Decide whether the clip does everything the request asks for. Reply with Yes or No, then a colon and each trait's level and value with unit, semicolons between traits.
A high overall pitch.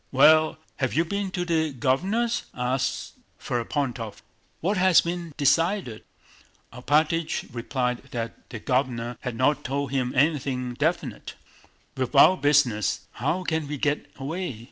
No: medium, 140 Hz